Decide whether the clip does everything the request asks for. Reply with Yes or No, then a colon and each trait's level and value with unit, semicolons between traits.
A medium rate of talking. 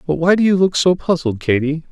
No: fast, 250 wpm